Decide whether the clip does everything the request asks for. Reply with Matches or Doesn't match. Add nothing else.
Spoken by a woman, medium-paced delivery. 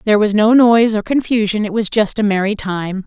Doesn't match